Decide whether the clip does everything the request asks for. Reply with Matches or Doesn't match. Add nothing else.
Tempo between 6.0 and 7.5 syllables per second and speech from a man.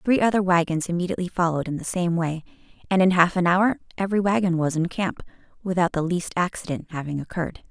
Doesn't match